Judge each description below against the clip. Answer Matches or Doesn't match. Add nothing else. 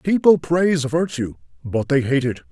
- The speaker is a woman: Doesn't match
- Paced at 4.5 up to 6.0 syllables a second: Matches